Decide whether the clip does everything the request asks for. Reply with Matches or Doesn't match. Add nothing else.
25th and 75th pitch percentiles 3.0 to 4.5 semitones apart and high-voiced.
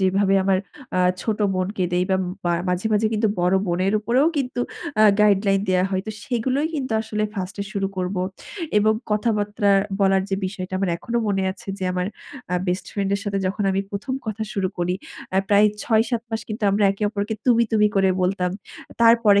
Doesn't match